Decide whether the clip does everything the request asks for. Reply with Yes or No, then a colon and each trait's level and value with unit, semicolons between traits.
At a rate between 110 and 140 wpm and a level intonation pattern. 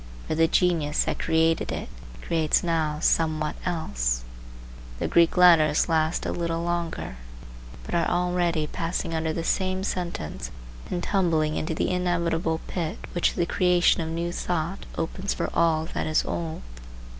No: average, 150 wpm; narrow, 1.7 semitones